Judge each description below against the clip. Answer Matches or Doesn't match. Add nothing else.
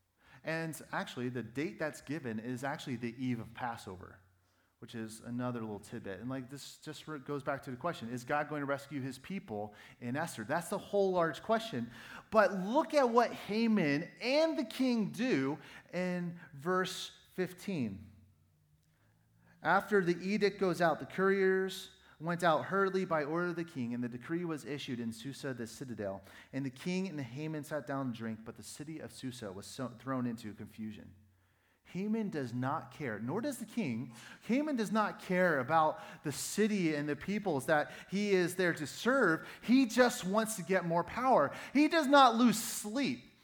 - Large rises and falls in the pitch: Matches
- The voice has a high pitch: Doesn't match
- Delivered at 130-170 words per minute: Doesn't match